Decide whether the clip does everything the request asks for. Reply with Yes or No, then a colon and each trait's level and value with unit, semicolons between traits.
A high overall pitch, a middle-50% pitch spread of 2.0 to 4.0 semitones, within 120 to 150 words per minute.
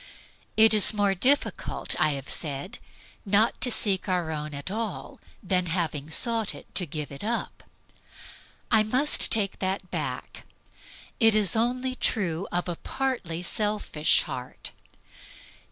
No: high, 195 Hz; average, 5.3 semitones; slow, 135 wpm